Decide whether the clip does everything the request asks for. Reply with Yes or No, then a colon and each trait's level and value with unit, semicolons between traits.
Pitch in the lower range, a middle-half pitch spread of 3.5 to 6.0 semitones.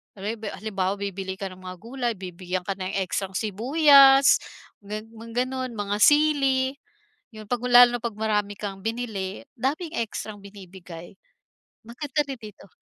No: high, 215 Hz; average, 4.3 semitones